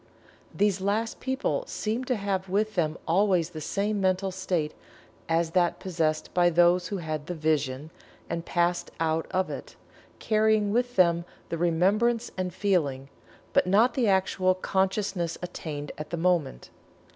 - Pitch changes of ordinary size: Yes, average, 3.5 semitones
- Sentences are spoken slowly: No, average, 150 wpm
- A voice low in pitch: No, medium, 180 Hz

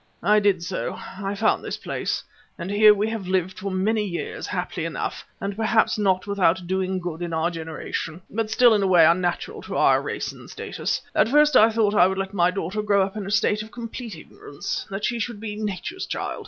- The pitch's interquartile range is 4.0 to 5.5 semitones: No, average, 2.8 semitones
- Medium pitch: No, high, 200 Hz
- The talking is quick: Yes, fast, 220 wpm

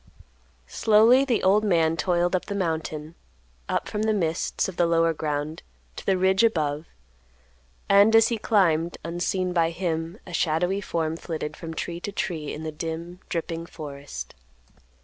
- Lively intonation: No, average, 3.2 semitones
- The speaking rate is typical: Yes, average, 160 wpm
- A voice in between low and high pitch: Yes, medium, 170 Hz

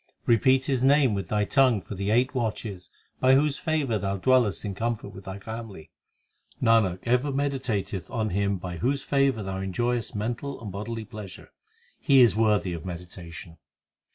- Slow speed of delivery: No, average, 170 wpm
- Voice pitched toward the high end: No, low, 110 Hz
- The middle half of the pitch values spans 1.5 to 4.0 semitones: No, average, 4.9 semitones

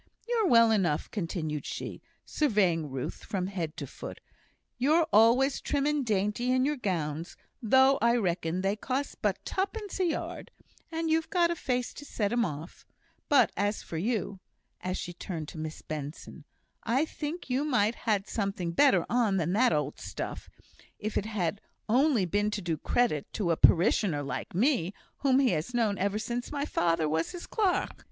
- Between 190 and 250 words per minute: No, average, 175 wpm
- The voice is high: Yes, high, 210 Hz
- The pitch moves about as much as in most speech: No, wide, 7.4 semitones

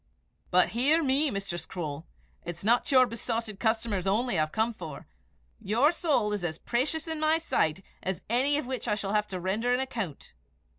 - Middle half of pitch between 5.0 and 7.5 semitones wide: Yes, wide, 5.6 semitones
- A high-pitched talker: Yes, high, 225 Hz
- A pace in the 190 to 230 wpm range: Yes, average, 195 wpm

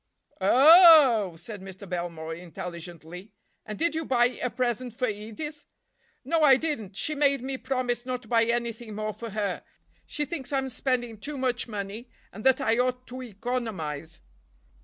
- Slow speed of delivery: No, average, 160 wpm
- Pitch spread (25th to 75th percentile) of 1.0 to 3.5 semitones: No, average, 4.5 semitones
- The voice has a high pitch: Yes, high, 240 Hz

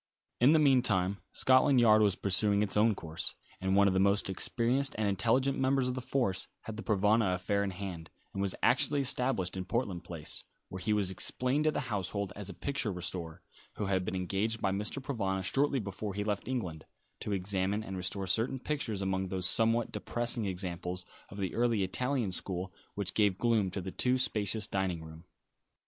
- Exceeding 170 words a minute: Yes, average, 190 wpm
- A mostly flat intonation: No, average, 3.9 semitones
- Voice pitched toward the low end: Yes, low, 100 Hz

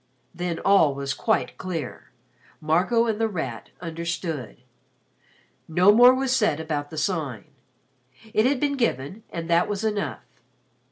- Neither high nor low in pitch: Yes, medium, 175 Hz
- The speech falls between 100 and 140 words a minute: Yes, slow, 135 wpm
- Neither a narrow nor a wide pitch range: No, wide, 6.0 semitones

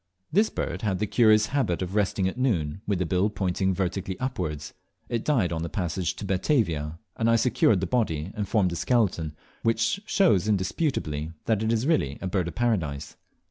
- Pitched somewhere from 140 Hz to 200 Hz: No, very low, 95 Hz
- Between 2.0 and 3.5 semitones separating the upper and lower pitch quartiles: No, average, 4.8 semitones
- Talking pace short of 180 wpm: No, average, 190 wpm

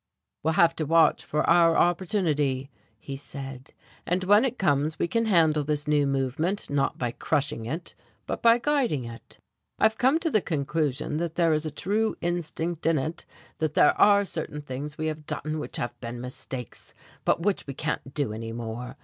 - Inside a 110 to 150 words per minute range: No, average, 185 wpm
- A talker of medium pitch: Yes, medium, 155 Hz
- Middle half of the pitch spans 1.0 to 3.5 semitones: No, average, 4.1 semitones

